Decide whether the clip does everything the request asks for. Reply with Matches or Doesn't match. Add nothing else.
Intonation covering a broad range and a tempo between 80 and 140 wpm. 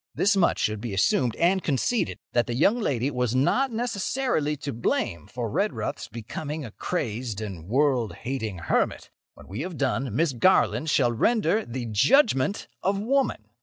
Doesn't match